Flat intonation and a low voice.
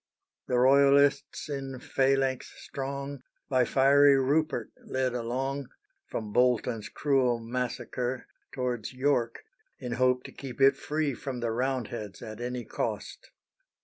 Yes: narrow, 2.0 semitones; low, 130 Hz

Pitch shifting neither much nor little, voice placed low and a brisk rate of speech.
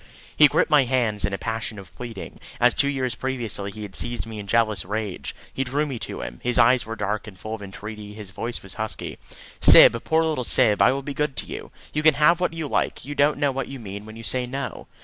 Yes: average, 4.4 semitones; low, 115 Hz; fast, 250 wpm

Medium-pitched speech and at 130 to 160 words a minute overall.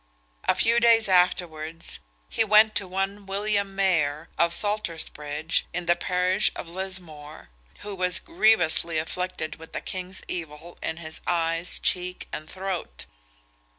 Yes: medium, 180 Hz; slow, 135 wpm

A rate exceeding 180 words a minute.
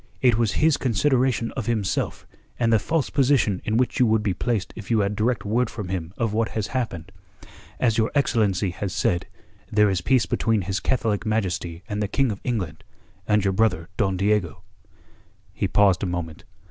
Yes: average, 190 wpm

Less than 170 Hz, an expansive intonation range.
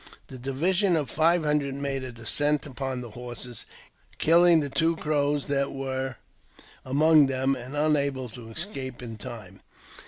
No: medium, 140 Hz; average, 2.8 semitones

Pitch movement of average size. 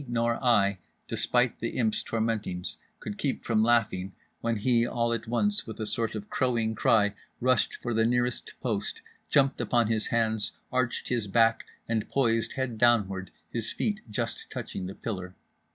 No: narrow, 2.1 semitones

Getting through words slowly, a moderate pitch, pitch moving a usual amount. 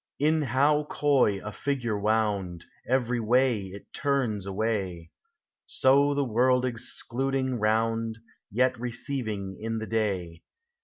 No: slow, 115 wpm; low, 115 Hz; average, 3.9 semitones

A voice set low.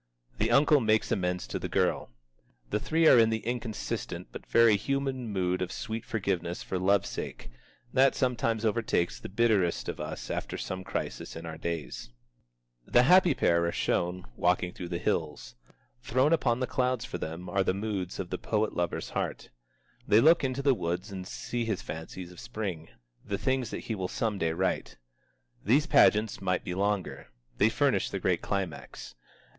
Yes: low, 105 Hz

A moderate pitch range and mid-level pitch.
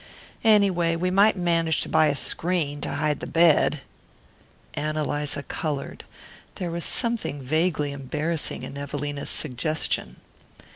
Yes: average, 3.0 semitones; medium, 155 Hz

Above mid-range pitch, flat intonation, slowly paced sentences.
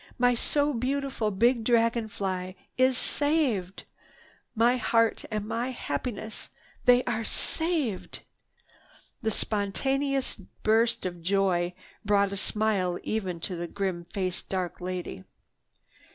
No: high, 220 Hz; average, 4.7 semitones; slow, 115 wpm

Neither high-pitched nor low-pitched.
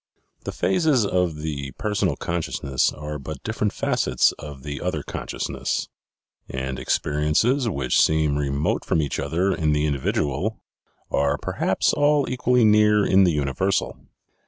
No: very low, 80 Hz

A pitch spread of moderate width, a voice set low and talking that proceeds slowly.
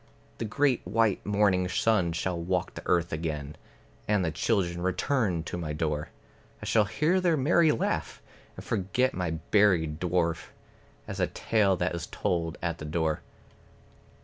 No: average, 4.4 semitones; very low, 90 Hz; average, 155 wpm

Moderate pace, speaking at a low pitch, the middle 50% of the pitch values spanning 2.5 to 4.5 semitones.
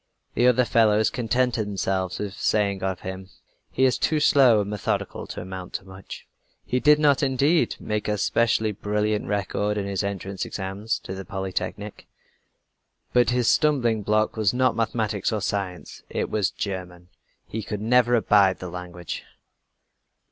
Yes: average, 155 wpm; low, 105 Hz; average, 3.6 semitones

